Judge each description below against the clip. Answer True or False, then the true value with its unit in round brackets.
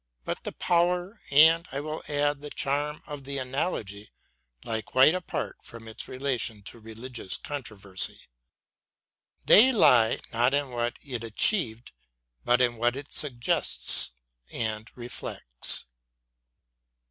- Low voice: True (125 Hz)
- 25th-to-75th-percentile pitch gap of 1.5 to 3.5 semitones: False (4.5 semitones)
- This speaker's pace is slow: True (130 wpm)